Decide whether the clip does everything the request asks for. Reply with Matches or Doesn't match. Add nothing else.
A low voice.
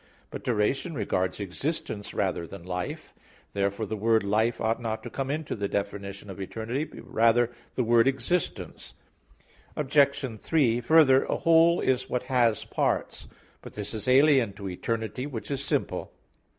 Matches